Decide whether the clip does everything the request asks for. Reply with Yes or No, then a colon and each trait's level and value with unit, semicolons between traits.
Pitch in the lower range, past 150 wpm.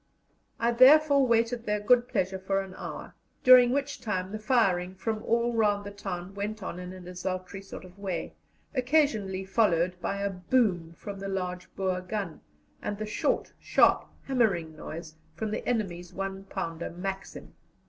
No: high, 195 Hz; average, 165 wpm